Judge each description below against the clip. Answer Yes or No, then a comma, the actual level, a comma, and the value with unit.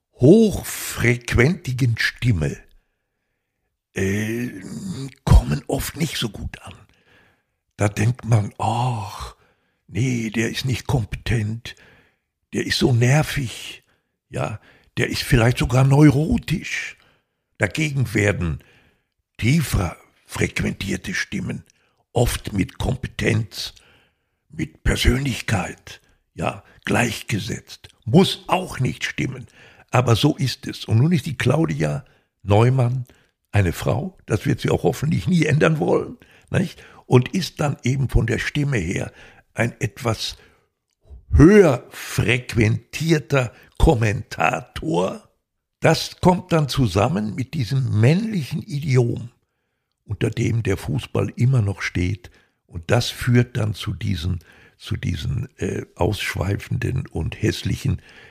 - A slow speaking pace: Yes, slow, 110 wpm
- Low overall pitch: Yes, low, 120 Hz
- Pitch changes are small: No, average, 4.5 semitones